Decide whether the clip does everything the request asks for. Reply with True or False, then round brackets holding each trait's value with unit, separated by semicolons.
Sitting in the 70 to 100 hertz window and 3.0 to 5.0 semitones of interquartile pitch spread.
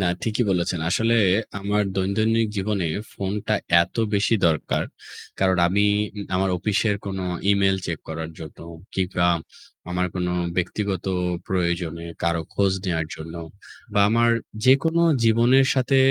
True (95 Hz; 3.7 semitones)